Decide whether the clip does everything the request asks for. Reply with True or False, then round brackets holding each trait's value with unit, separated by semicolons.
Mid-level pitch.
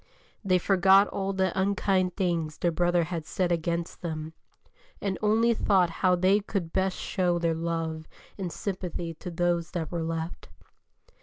True (175 Hz)